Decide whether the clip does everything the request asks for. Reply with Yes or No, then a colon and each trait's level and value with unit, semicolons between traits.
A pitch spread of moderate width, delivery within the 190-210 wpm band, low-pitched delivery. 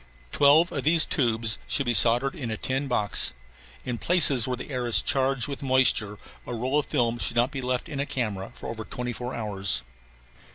Yes: average, 3.0 semitones; average, 200 wpm; low, 125 Hz